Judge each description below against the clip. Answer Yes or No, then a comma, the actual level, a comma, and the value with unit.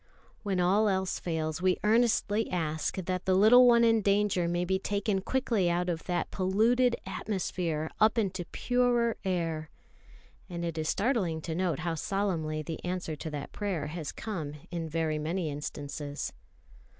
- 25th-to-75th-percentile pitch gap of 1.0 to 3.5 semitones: No, average, 4.3 semitones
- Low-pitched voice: No, medium, 185 Hz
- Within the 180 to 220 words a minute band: No, average, 160 wpm